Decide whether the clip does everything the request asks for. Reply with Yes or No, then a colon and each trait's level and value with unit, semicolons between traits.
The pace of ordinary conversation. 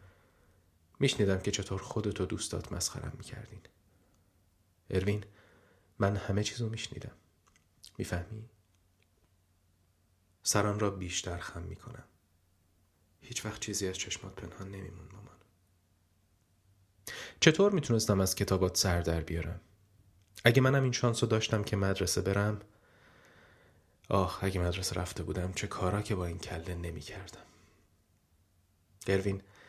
Yes: average, 115 wpm